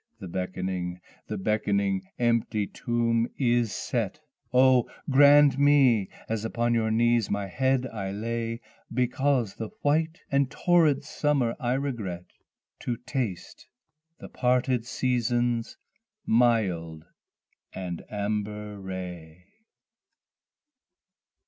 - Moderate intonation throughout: Yes, average, 4.2 semitones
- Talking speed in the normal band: No, slow, 100 wpm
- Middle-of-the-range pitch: No, low, 115 Hz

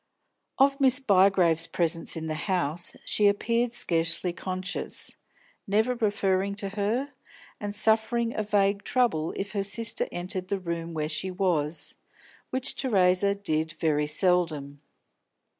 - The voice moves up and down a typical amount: Yes, average, 4.2 semitones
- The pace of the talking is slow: Yes, slow, 130 wpm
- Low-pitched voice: No, high, 190 Hz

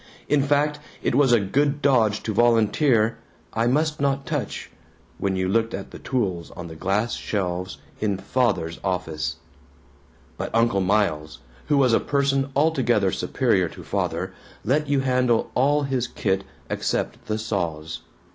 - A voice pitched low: Yes, low, 115 Hz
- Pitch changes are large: Yes, wide, 6.1 semitones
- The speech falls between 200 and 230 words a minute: No, average, 150 wpm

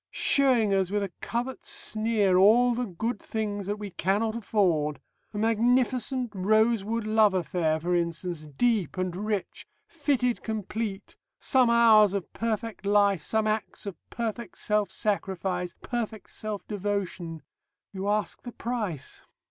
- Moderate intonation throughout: Yes, average, 3.3 semitones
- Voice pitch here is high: Yes, high, 210 Hz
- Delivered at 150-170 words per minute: No, slow, 135 wpm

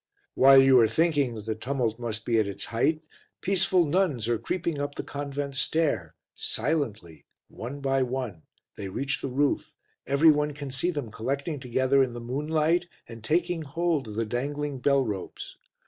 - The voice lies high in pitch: No, low, 135 Hz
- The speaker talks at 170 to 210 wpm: Yes, average, 175 wpm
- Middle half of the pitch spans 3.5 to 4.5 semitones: Yes, average, 4.1 semitones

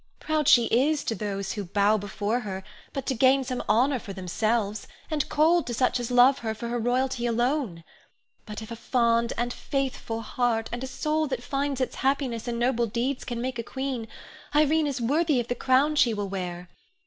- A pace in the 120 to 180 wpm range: No, average, 200 wpm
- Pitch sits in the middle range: No, high, 240 Hz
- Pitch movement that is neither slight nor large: Yes, average, 3.2 semitones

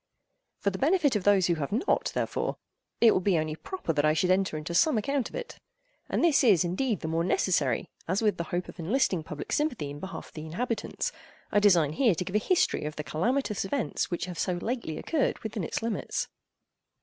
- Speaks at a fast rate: Yes, fast, 220 wpm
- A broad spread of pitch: Yes, wide, 6.5 semitones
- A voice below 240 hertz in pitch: Yes, high, 190 Hz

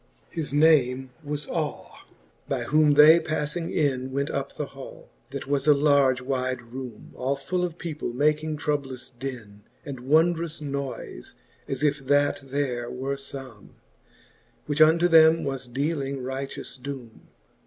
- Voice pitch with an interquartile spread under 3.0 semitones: Yes, narrow, 2.6 semitones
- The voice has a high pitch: No, medium, 140 Hz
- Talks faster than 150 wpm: No, average, 145 wpm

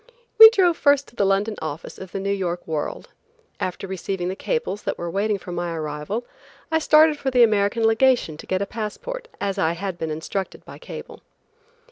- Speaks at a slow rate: No, average, 195 wpm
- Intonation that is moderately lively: No, wide, 5.9 semitones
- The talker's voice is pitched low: No, high, 200 Hz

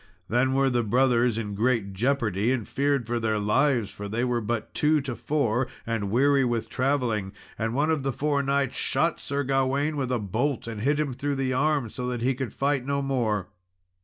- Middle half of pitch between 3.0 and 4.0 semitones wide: Yes, average, 3.6 semitones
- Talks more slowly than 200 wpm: No, fast, 205 wpm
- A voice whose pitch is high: No, low, 125 Hz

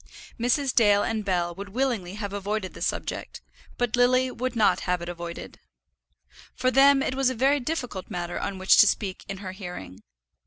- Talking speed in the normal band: Yes, average, 185 wpm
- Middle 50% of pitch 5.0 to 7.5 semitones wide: Yes, average, 5.3 semitones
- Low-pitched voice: No, high, 210 Hz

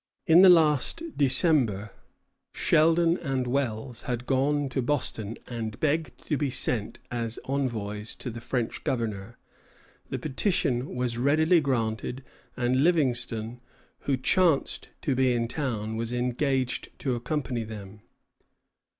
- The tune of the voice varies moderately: Yes, average, 3.9 semitones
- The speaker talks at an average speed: No, slow, 130 wpm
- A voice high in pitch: No, low, 125 Hz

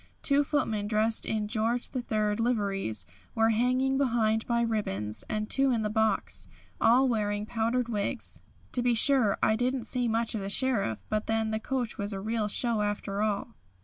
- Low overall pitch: No, high, 220 Hz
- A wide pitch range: No, narrow, 2.5 semitones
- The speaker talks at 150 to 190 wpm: Yes, average, 180 wpm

